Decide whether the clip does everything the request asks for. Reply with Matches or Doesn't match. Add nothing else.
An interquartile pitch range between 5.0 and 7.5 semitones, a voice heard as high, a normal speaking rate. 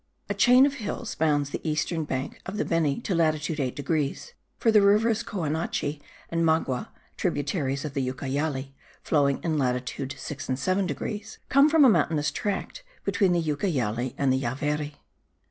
Doesn't match